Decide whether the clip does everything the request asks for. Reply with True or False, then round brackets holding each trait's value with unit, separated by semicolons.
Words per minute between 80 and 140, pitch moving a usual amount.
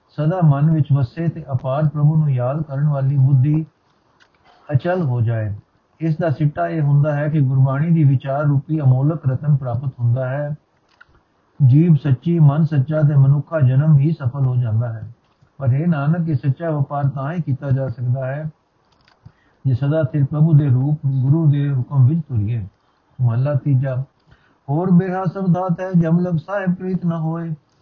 False (165 wpm; 3.2 semitones)